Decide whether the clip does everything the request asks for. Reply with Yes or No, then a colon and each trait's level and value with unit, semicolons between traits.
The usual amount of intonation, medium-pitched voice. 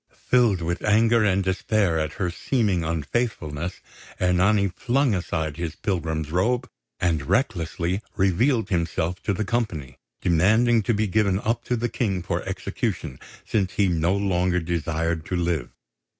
No: average, 4.4 semitones; very low, 95 Hz